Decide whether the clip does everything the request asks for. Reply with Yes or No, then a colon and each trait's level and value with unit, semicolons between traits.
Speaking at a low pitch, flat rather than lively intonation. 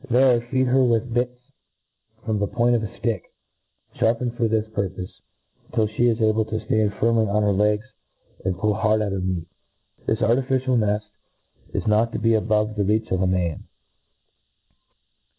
Yes: low, 110 Hz; narrow, 2.2 semitones